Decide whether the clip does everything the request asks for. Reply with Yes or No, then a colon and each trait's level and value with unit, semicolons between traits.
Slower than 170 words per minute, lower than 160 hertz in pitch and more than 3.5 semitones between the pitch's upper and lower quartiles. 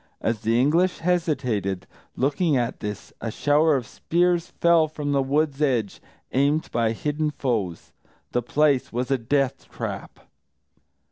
Yes: average, 140 wpm; medium, 140 Hz; average, 4.7 semitones